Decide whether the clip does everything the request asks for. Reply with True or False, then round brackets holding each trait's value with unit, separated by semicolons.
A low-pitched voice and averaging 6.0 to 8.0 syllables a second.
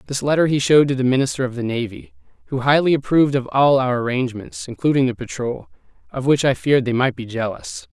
True (130 Hz; 6.4 syllables/s)